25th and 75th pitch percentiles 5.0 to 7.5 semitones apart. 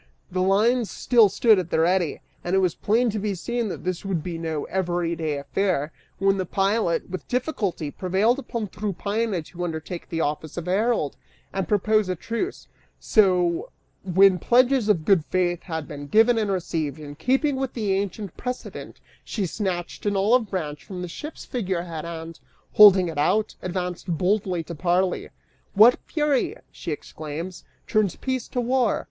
No: average, 4.2 semitones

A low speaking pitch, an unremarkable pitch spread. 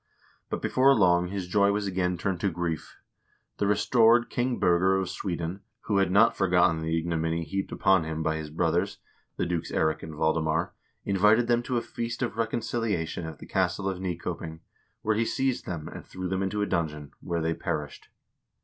Yes: very low, 90 Hz; average, 3.9 semitones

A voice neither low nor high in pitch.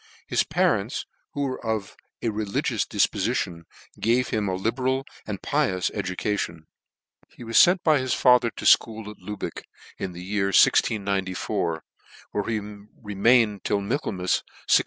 No: low, 105 Hz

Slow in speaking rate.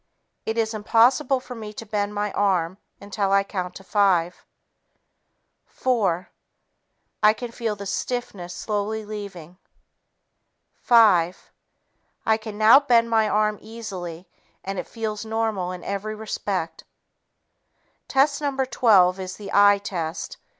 Yes: slow, 130 wpm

